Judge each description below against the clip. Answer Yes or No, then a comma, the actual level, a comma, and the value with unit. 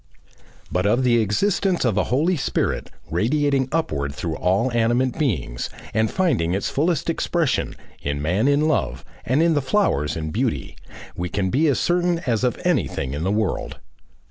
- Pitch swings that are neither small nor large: No, wide, 9.0 semitones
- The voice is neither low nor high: No, low, 120 Hz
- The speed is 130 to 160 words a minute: No, average, 170 wpm